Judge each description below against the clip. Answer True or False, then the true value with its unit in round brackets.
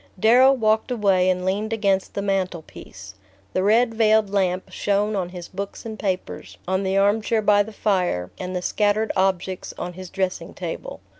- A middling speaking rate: True (175 wpm)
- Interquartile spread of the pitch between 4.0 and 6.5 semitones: False (2.6 semitones)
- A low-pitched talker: False (195 Hz)